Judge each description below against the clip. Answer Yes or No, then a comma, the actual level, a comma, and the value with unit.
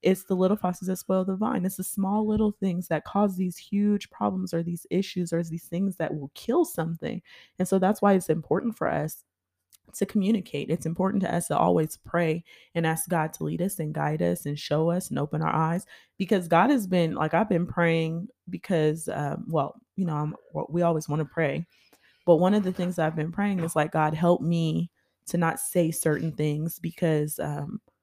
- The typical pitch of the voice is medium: Yes, medium, 170 Hz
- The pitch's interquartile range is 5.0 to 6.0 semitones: No, average, 3.1 semitones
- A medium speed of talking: No, fast, 215 wpm